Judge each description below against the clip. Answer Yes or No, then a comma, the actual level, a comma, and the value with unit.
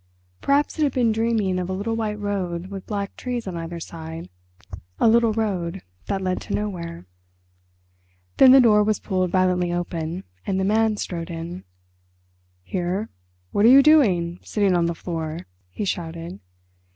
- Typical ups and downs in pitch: Yes, average, 4.1 semitones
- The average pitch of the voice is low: No, high, 190 Hz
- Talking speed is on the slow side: No, average, 165 wpm